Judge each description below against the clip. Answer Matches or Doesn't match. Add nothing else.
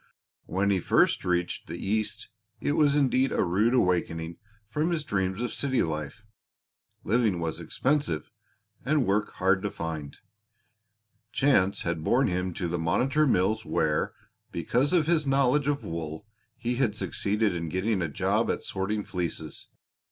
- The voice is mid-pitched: Doesn't match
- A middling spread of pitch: Doesn't match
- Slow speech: Doesn't match